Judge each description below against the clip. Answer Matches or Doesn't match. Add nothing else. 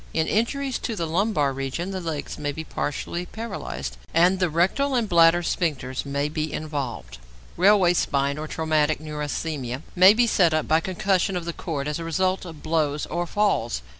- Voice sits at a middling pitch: Matches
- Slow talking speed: Doesn't match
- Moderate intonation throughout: Matches